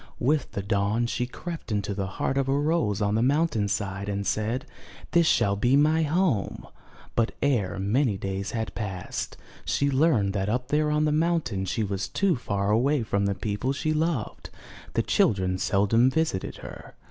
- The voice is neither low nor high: No, low, 115 Hz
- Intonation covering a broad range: Yes, wide, 6.5 semitones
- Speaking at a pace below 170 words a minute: No, average, 180 wpm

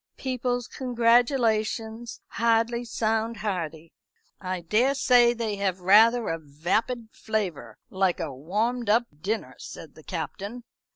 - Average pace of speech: No, slow, 115 wpm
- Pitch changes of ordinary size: Yes, average, 4.1 semitones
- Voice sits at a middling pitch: No, high, 220 Hz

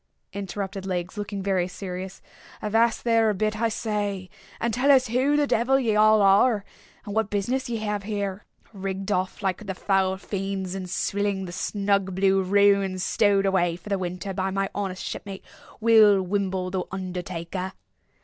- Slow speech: No, average, 170 wpm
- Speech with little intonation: Yes, narrow, 2.1 semitones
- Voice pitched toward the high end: Yes, high, 195 Hz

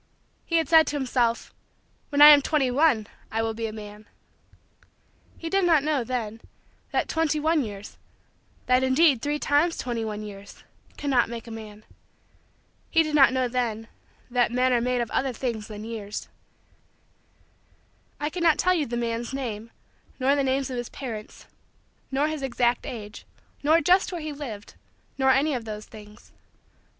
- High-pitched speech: Yes, very high, 255 Hz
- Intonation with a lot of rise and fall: No, average, 4.7 semitones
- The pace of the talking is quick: No, average, 170 wpm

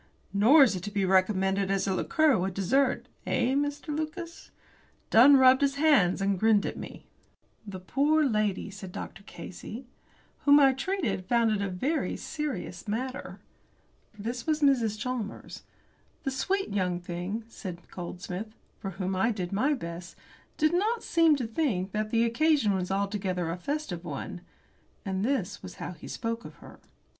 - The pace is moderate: Yes, average, 165 wpm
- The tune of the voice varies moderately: No, wide, 6.6 semitones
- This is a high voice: Yes, high, 215 Hz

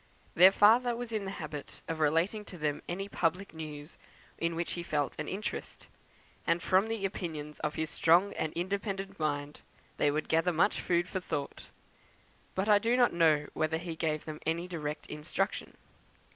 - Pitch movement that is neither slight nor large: Yes, average, 4.1 semitones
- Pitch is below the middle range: No, medium, 170 Hz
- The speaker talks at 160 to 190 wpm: Yes, average, 175 wpm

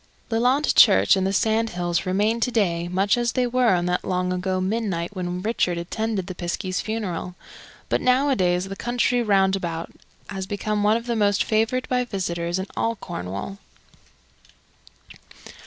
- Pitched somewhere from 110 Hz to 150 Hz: No, high, 195 Hz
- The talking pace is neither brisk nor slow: Yes, average, 160 wpm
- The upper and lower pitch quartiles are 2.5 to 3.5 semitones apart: No, average, 4.0 semitones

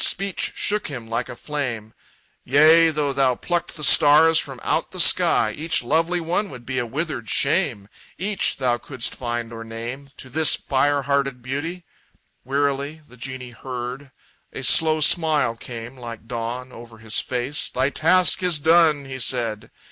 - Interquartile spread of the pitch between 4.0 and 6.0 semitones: Yes, average, 4.5 semitones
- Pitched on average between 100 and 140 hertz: Yes, low, 135 Hz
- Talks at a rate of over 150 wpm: Yes, average, 165 wpm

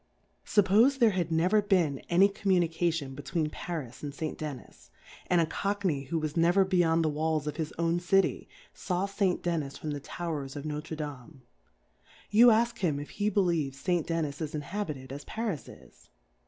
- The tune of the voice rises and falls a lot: No, average, 4.2 semitones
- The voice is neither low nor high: Yes, medium, 165 Hz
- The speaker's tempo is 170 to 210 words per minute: Yes, average, 185 wpm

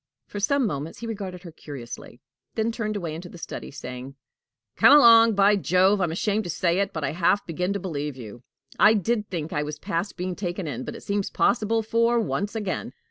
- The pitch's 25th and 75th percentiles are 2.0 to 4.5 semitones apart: No, average, 4.9 semitones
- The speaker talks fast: Yes, fast, 215 wpm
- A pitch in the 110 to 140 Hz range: No, medium, 185 Hz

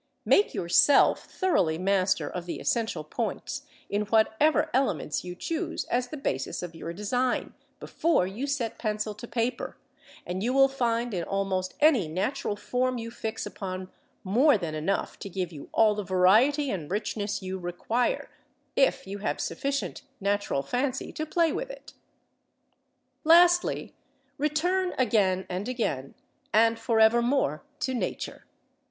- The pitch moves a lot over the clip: Yes, wide, 5.8 semitones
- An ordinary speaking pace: Yes, average, 145 wpm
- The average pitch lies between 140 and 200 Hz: No, high, 220 Hz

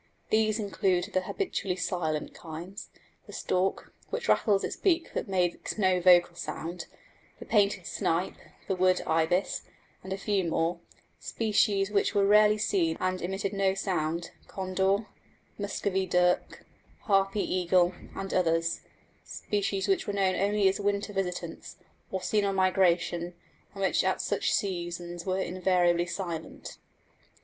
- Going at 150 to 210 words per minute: No, average, 140 wpm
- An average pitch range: No, narrow, 2.2 semitones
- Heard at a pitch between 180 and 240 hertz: Yes, high, 190 Hz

